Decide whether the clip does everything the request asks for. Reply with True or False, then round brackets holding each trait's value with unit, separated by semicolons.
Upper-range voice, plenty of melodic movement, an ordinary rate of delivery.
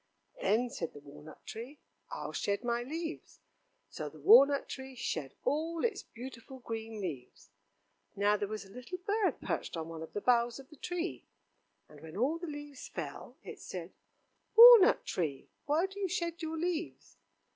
True (255 Hz; 8.6 semitones; 170 wpm)